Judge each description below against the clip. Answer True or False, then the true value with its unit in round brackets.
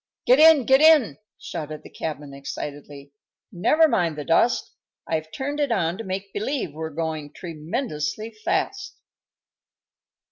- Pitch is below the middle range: False (175 Hz)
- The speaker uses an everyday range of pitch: False (8.9 semitones)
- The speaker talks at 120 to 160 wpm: True (135 wpm)